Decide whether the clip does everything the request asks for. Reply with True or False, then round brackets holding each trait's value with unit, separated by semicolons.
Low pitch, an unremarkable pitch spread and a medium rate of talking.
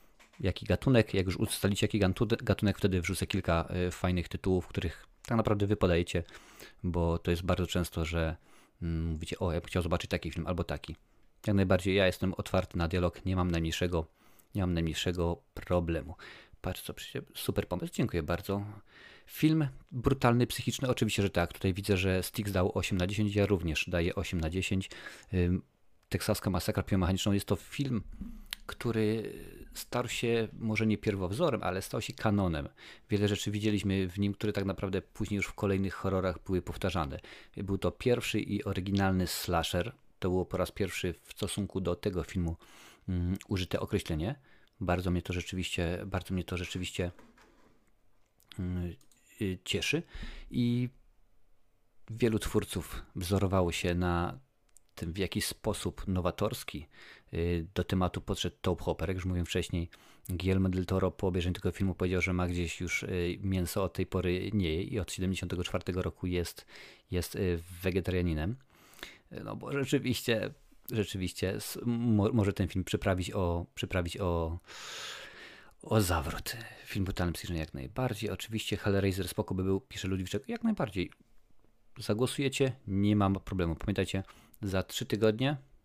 True (95 Hz; 3.0 semitones; 150 wpm)